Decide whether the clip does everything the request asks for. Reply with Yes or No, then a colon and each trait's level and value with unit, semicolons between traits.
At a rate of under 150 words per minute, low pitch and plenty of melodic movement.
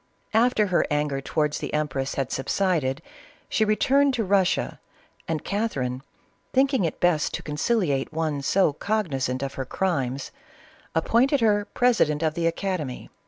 No: average, 140 wpm; medium, 165 Hz; wide, 7.1 semitones